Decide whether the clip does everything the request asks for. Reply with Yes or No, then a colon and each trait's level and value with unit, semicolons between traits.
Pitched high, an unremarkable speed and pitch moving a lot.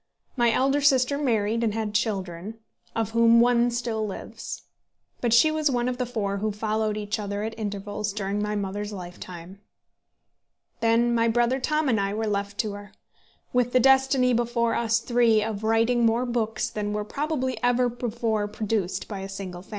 No: high, 225 Hz; average, 180 wpm; average, 2.7 semitones